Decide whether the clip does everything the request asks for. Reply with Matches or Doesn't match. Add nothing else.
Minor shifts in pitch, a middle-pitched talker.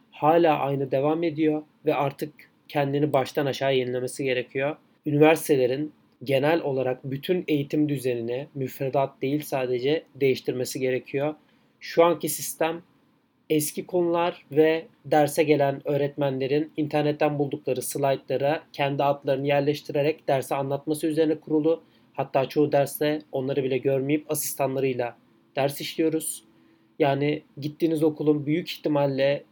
Matches